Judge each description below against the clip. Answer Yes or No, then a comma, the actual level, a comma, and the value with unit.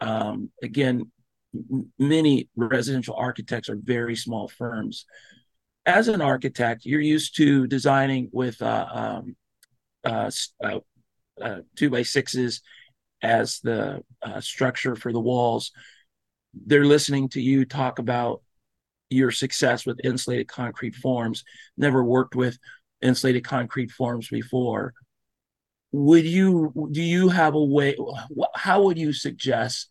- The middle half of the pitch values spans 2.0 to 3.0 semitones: Yes, average, 2.7 semitones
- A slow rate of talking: Yes, slow, 125 wpm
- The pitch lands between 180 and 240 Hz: No, low, 130 Hz